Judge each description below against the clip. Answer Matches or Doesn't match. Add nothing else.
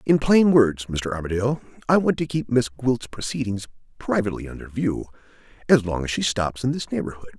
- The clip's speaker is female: Doesn't match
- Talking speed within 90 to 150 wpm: Doesn't match